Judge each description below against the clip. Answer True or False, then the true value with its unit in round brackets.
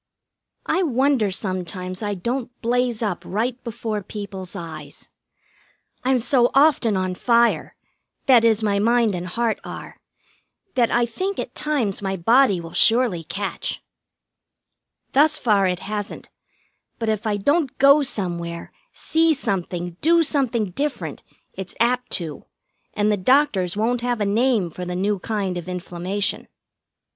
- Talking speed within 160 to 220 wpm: False (140 wpm)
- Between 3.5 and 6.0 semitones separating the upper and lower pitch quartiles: True (5.0 semitones)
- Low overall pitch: False (215 Hz)